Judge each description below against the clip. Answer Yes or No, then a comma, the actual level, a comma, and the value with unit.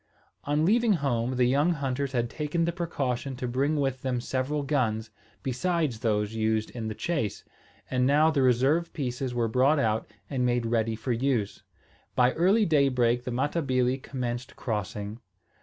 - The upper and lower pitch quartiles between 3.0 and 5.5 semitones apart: Yes, average, 3.5 semitones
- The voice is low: Yes, low, 130 Hz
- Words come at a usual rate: Yes, average, 160 wpm